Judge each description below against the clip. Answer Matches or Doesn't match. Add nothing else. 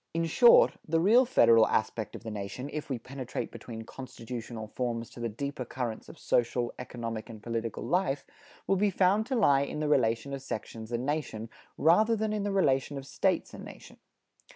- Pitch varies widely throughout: Matches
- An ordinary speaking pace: Matches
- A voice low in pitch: Matches